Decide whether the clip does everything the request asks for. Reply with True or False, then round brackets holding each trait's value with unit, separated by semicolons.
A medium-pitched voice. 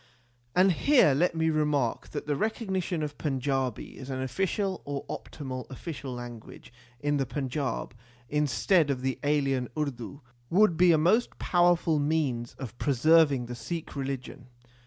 True (145 Hz)